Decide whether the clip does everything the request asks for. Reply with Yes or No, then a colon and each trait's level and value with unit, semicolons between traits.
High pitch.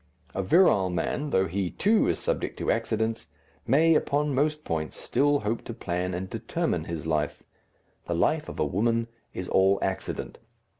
No: low, 105 Hz